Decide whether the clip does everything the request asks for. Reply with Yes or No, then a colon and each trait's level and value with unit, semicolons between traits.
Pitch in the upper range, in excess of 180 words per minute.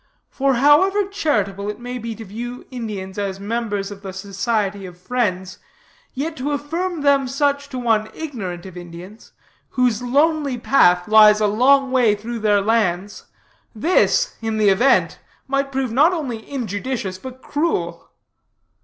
No: high, 235 Hz; average, 150 wpm